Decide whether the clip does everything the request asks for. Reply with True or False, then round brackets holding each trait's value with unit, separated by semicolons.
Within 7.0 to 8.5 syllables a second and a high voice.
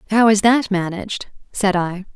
False (4.9 syllables/s; 200 Hz)